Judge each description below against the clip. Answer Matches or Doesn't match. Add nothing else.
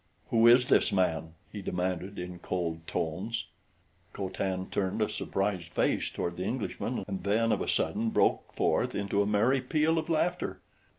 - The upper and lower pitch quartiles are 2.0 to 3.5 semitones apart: Doesn't match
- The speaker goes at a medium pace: Matches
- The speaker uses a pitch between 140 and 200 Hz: Doesn't match